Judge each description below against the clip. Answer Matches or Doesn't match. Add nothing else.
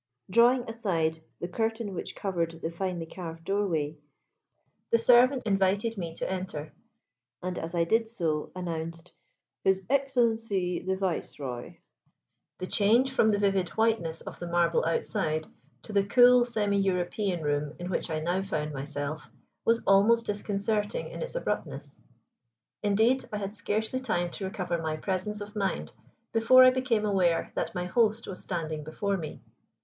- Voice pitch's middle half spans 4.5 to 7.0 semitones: Matches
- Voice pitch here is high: Matches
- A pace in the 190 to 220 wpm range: Doesn't match